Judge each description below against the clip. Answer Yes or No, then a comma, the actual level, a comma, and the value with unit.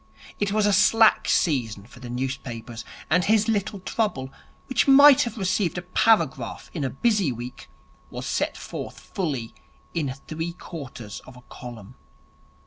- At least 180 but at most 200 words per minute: No, average, 150 wpm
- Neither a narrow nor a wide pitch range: No, wide, 8.7 semitones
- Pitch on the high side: No, medium, 160 Hz